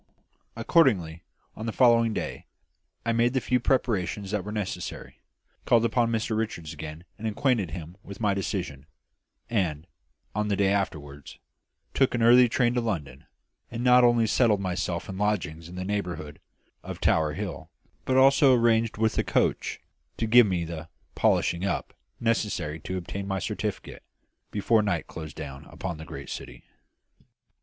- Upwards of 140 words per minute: Yes, average, 160 wpm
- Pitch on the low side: Yes, low, 100 Hz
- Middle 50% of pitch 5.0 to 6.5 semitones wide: Yes, average, 5.3 semitones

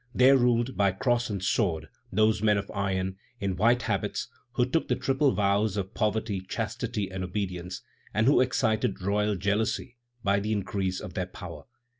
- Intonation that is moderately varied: Yes, average, 3.3 semitones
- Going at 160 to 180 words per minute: Yes, average, 170 wpm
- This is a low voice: Yes, low, 105 Hz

